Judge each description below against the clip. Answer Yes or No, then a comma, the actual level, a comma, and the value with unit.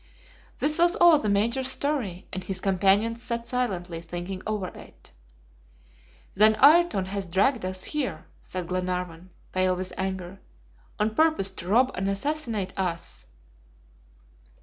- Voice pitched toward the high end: Yes, high, 195 Hz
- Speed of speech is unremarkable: No, slow, 130 wpm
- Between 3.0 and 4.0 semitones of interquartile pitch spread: No, average, 5.1 semitones